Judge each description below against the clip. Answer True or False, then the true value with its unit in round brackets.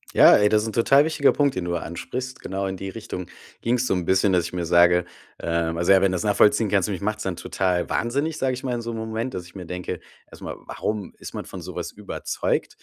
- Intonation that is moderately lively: True (4.6 semitones)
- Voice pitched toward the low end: True (100 Hz)